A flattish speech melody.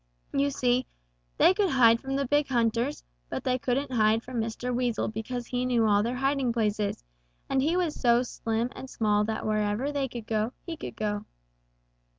No: average, 3.2 semitones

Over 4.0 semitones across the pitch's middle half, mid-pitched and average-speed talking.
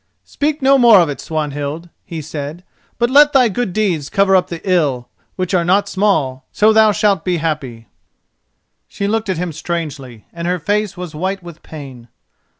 Yes: average, 5.2 semitones; medium, 175 Hz; average, 180 wpm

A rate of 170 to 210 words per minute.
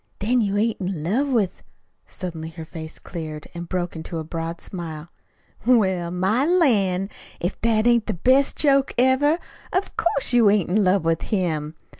Yes: average, 175 wpm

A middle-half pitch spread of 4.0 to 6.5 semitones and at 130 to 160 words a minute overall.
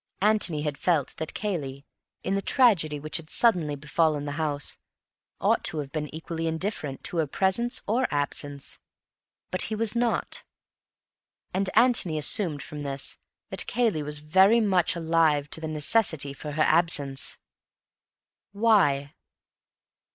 Yes: average, 5.1 semitones; average, 140 wpm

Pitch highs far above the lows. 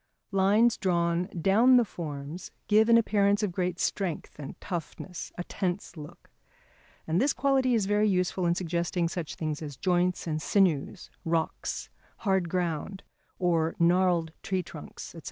No: average, 3.2 semitones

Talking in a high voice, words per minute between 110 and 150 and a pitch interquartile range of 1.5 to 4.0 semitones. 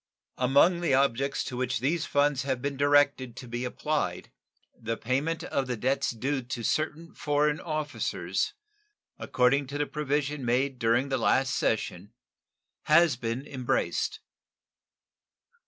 No: low, 135 Hz; slow, 135 wpm; average, 2.7 semitones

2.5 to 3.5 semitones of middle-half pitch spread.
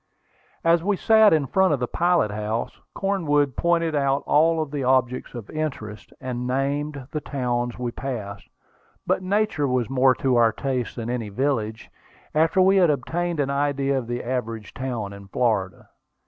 No: average, 4.5 semitones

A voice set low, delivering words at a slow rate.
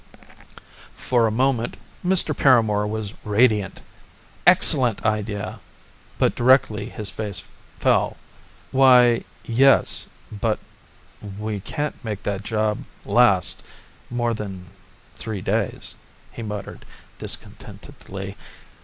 Yes: low, 110 Hz; slow, 95 wpm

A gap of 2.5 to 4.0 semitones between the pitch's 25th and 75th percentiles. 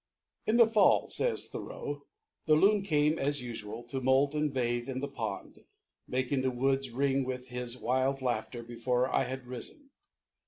Yes: average, 2.8 semitones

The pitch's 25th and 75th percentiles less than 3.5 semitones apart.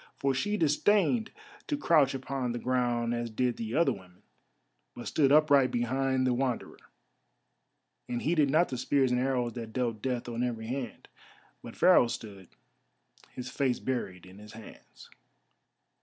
Yes: narrow, 2.6 semitones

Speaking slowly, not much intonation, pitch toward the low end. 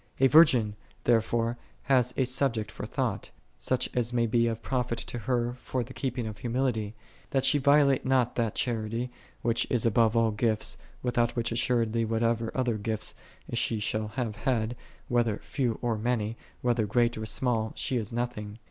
No: average, 175 wpm; narrow, 2.0 semitones; low, 120 Hz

